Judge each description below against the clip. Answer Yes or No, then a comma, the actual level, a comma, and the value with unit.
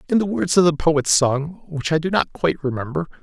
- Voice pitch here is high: No, medium, 160 Hz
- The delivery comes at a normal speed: No, fast, 240 wpm